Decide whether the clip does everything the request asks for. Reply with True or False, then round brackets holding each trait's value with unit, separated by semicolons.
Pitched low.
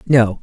True (120 Hz)